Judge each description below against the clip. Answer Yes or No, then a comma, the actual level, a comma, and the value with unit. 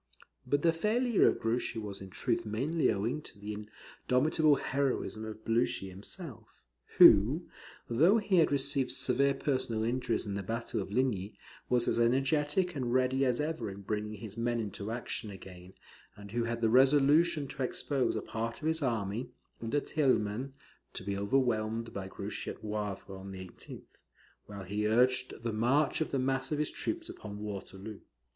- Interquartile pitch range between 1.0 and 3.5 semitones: No, average, 4.7 semitones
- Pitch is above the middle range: No, low, 120 Hz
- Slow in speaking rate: No, average, 170 wpm